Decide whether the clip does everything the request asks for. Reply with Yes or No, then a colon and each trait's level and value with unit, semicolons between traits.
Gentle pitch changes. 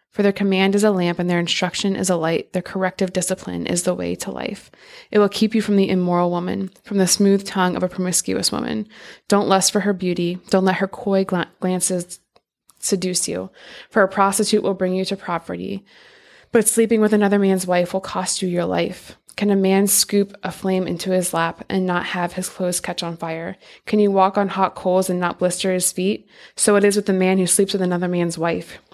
Yes: narrow, 1.9 semitones